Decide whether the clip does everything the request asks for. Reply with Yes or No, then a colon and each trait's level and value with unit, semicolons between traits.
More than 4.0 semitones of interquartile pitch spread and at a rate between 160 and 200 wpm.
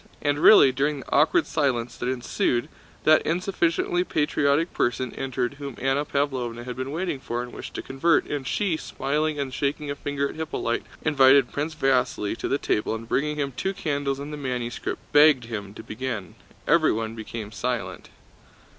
No: average, 3.3 semitones; average, 170 wpm